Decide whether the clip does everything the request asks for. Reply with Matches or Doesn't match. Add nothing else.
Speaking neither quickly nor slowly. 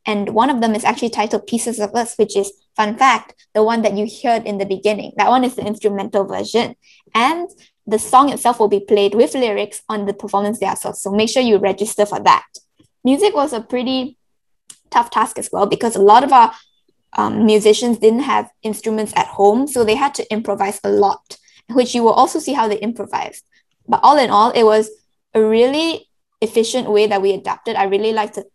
Doesn't match